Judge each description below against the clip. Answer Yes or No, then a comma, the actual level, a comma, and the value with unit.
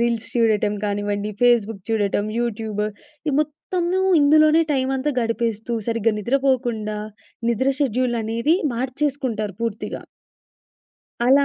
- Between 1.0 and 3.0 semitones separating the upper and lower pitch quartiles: No, average, 3.8 semitones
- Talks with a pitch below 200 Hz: No, high, 235 Hz